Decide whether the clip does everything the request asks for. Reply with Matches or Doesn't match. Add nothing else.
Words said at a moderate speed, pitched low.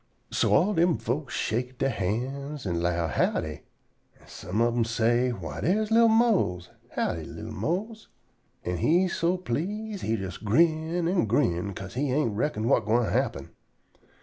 Matches